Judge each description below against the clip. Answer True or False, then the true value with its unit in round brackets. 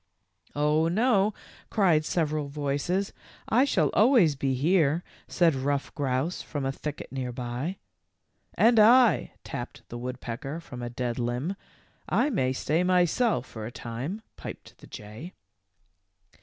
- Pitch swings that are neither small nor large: False (6.2 semitones)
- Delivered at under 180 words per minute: True (150 wpm)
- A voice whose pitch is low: False (150 Hz)